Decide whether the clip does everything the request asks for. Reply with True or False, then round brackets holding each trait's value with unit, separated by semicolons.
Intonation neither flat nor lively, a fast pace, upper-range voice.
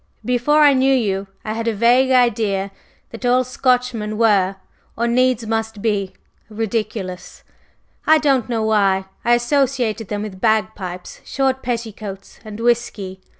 False (3.2 semitones; 140 wpm; 225 Hz)